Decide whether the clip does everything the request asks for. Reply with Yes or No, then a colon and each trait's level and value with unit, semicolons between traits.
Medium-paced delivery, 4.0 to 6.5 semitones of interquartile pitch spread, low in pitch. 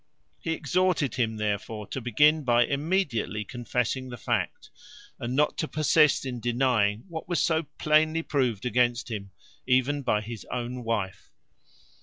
Yes: average, 145 wpm; average, 4.7 semitones; low, 125 Hz